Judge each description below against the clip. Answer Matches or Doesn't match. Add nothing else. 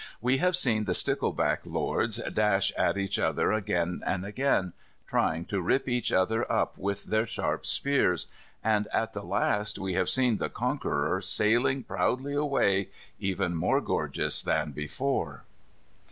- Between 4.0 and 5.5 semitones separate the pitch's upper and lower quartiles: Matches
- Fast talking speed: Doesn't match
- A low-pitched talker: Matches